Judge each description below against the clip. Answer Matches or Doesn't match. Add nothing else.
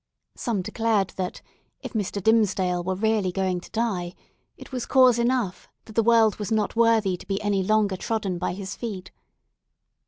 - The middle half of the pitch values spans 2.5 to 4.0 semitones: Matches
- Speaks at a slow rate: Doesn't match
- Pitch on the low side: Doesn't match